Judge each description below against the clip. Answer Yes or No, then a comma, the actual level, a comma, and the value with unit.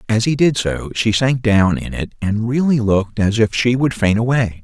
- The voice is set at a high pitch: No, low, 115 Hz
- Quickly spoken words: Yes, fast, 235 wpm